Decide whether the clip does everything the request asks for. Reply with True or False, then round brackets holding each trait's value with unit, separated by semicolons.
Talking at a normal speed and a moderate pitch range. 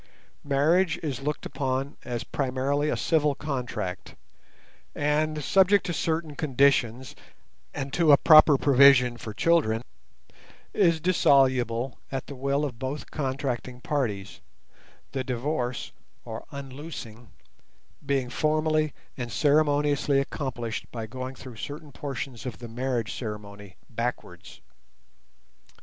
False (115 wpm; 3.4 semitones)